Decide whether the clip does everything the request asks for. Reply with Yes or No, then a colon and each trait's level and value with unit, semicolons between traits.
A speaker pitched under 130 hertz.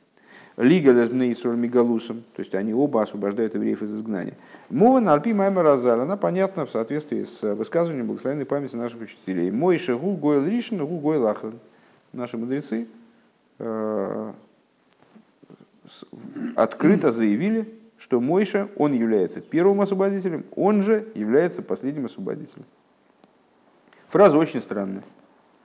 No: low, 135 Hz